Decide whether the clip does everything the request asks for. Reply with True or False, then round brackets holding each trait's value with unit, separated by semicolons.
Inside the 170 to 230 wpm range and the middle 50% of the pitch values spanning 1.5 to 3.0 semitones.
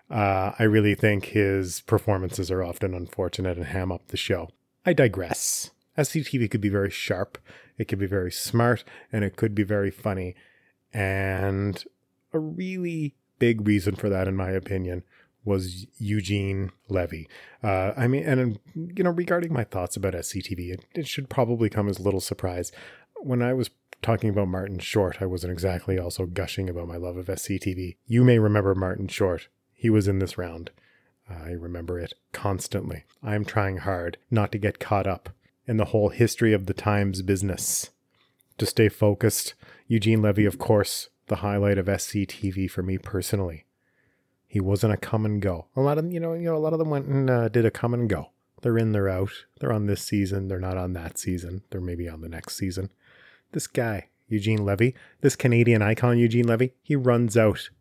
False (190 wpm; 3.7 semitones)